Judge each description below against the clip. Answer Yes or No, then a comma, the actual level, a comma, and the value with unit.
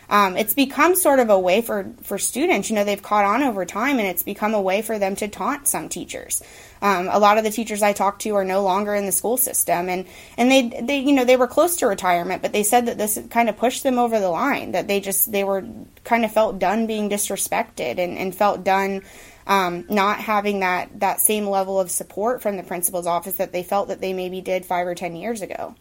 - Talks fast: Yes, fast, 250 wpm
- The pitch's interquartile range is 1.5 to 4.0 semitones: Yes, average, 3.4 semitones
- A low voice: No, high, 205 Hz